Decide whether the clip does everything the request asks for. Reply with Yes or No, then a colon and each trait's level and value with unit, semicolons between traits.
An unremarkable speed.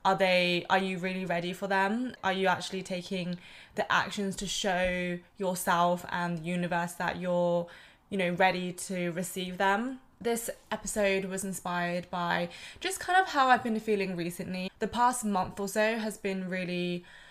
Yes: average, 170 wpm